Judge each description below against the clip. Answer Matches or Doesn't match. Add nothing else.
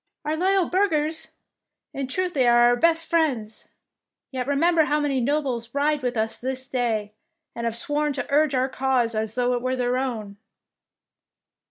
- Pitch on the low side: Doesn't match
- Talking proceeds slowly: Doesn't match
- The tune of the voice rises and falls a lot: Doesn't match